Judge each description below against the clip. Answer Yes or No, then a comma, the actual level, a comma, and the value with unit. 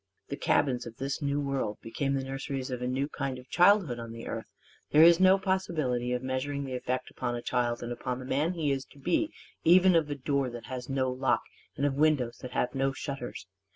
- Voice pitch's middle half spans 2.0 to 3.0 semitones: Yes, average, 2.7 semitones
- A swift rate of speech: Yes, fast, 225 wpm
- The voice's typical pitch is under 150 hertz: Yes, low, 135 Hz